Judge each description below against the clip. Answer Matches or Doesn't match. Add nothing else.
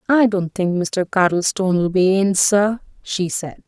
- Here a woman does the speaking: Matches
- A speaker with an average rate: Matches